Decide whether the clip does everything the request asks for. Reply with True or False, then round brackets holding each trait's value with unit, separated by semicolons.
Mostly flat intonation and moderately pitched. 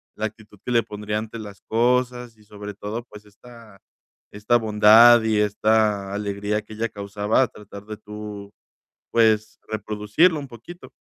False (1.9 semitones; 105 Hz)